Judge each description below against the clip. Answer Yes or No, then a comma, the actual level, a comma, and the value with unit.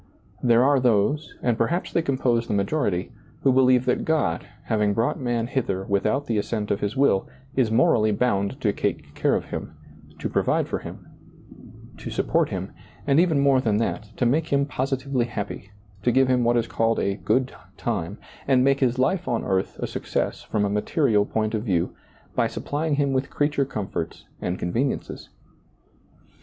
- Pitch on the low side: Yes, low, 120 Hz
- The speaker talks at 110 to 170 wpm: No, average, 180 wpm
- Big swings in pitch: No, average, 4.6 semitones